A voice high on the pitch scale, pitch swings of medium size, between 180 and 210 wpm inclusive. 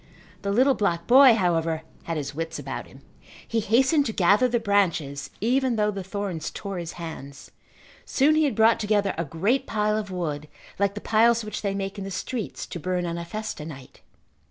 Yes: high, 200 Hz; average, 4.8 semitones; average, 200 wpm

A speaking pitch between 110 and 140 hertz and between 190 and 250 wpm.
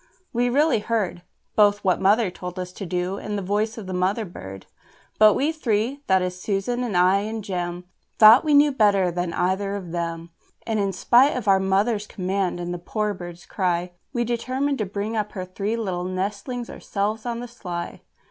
No: high, 200 Hz; average, 195 wpm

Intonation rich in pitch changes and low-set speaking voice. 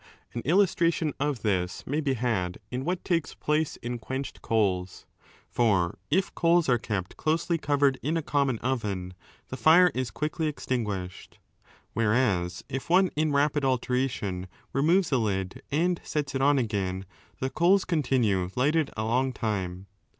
Yes: wide, 6.6 semitones; low, 130 Hz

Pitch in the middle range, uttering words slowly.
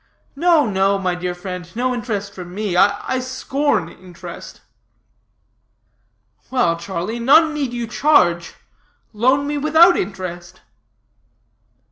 No: high, 210 Hz; slow, 110 wpm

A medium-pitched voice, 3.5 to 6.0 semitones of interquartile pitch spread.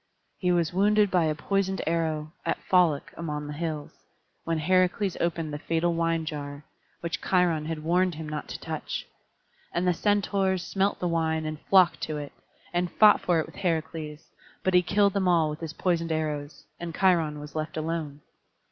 No: medium, 165 Hz; average, 2.8 semitones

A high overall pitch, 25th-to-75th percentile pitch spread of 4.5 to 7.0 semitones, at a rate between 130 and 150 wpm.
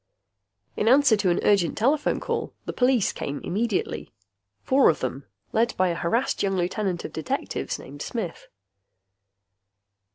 Yes: high, 200 Hz; wide, 5.5 semitones; average, 140 wpm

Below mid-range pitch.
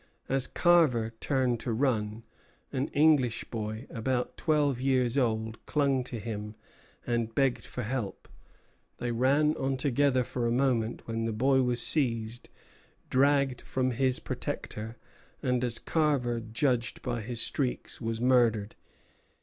Yes: low, 125 Hz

